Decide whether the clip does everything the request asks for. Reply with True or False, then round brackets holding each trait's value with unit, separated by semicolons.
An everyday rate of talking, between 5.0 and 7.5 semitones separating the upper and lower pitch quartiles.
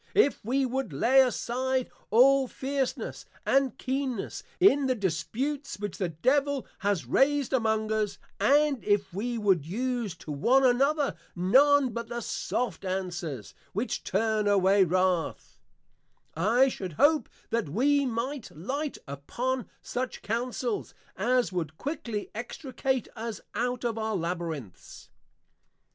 False (125 wpm; 5.3 semitones)